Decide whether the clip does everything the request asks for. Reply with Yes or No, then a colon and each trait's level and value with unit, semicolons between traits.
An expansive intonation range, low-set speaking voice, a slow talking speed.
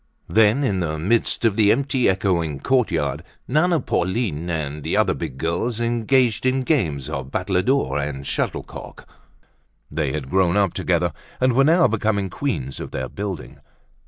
No: wide, 7.7 semitones; low, 100 Hz; average, 150 wpm